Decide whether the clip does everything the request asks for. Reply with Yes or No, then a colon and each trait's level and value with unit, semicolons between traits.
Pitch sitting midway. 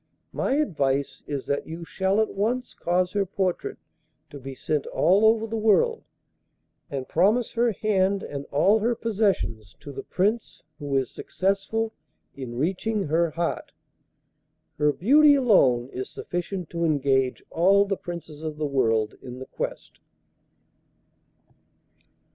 Yes: medium, 175 Hz